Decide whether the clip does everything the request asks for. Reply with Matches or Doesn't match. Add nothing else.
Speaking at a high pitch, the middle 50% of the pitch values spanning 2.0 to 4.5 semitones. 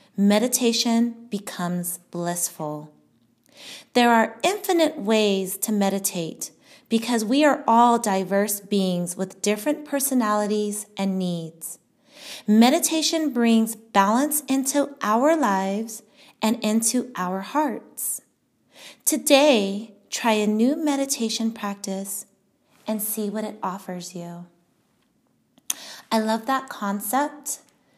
Doesn't match